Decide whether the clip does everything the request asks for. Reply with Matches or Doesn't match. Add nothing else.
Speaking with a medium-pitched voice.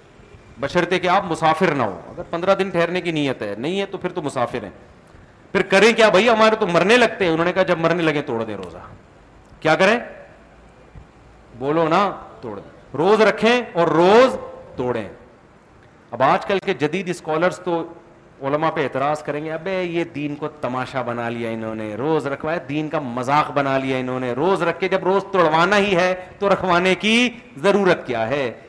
Matches